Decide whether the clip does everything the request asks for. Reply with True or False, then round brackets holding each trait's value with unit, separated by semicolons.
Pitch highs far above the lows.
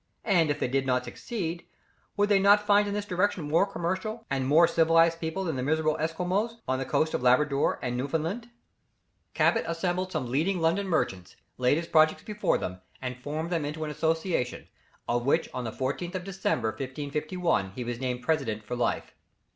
True (5.9 semitones)